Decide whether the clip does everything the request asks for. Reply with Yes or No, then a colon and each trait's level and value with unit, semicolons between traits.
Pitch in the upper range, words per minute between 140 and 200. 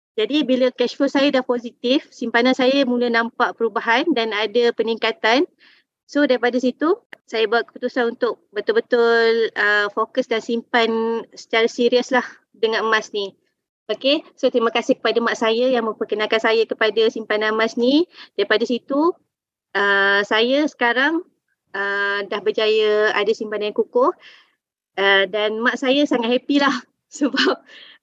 Yes: high, 235 Hz; average, 145 wpm